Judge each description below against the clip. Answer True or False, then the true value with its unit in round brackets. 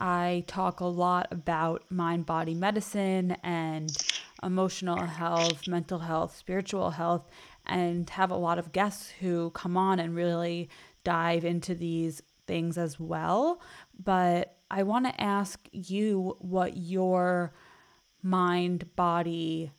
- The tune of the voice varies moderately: False (2.0 semitones)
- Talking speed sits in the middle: False (125 wpm)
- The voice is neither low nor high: True (175 Hz)